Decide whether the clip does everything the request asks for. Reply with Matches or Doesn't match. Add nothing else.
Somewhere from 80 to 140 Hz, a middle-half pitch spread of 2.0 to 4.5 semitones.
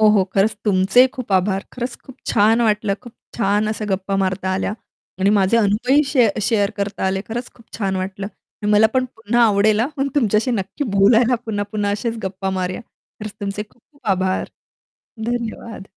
Doesn't match